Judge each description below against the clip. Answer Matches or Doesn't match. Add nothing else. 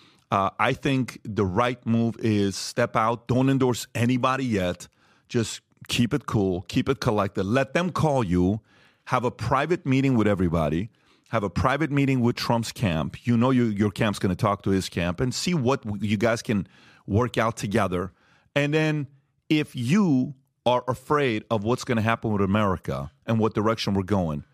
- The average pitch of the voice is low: Matches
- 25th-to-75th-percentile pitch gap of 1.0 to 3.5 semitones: Doesn't match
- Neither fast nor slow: Matches